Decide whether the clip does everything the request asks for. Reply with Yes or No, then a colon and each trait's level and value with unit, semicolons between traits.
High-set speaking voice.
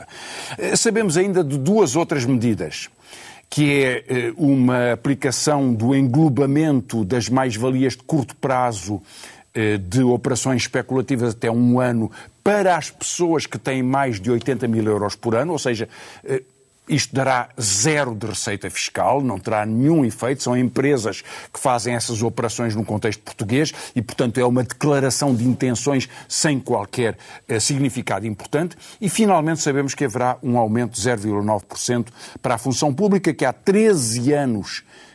No: low, 130 Hz